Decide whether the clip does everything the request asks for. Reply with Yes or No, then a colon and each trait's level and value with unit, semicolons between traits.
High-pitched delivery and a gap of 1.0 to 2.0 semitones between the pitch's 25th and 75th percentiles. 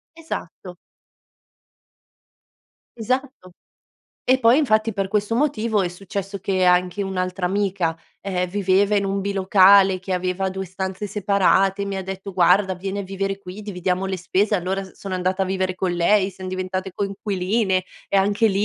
Yes: high, 195 Hz; narrow, 1.5 semitones